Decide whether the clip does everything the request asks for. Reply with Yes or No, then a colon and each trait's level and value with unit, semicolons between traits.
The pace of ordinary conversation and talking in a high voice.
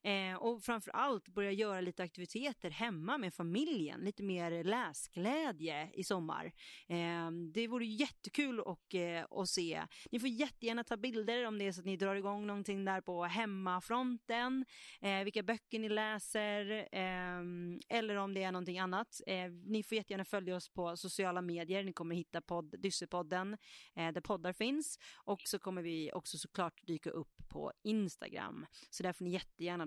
Yes: average, 155 wpm; high, 195 Hz